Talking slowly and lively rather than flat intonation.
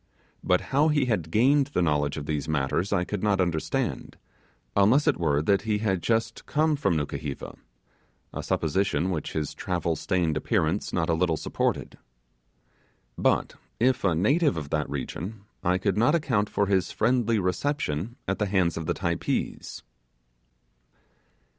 No: average, 155 wpm; wide, 5.8 semitones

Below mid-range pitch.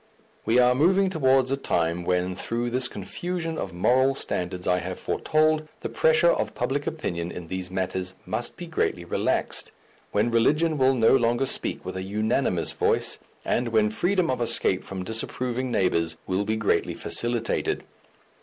Yes: low, 120 Hz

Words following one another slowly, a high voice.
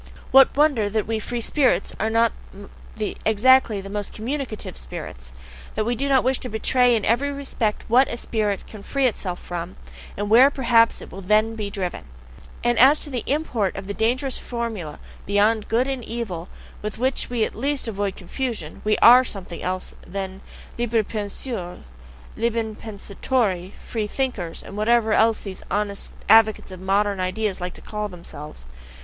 No: average, 165 wpm; high, 220 Hz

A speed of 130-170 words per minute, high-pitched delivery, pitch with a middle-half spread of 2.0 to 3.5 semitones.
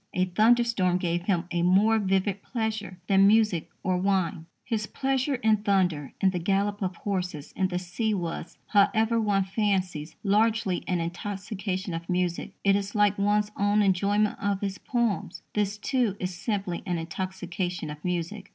Yes: average, 160 wpm; high, 195 Hz; narrow, 2.6 semitones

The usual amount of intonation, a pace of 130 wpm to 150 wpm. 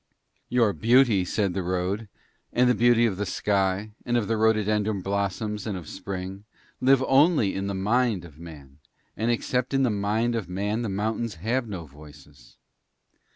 No: average, 3.8 semitones; average, 170 wpm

